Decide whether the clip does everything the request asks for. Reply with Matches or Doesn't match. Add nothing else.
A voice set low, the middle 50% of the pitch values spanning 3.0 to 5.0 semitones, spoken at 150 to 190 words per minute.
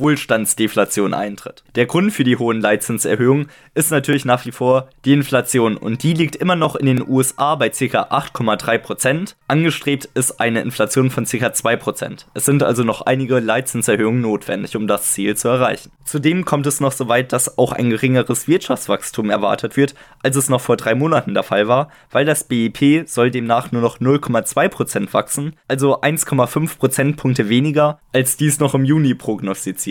Matches